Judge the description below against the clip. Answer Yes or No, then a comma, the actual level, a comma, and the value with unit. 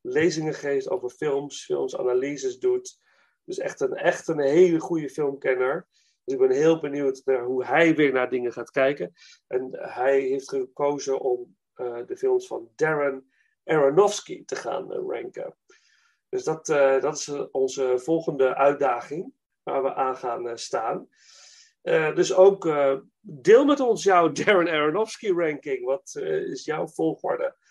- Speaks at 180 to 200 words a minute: No, average, 155 wpm